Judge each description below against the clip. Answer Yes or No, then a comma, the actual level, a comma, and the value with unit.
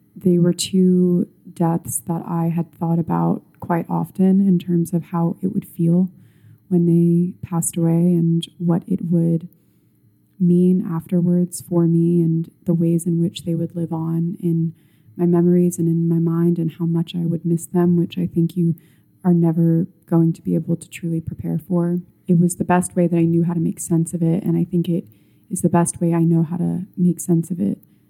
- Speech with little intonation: Yes, narrow, 1.0 semitones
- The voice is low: No, medium, 170 Hz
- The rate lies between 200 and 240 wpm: Yes, fast, 205 wpm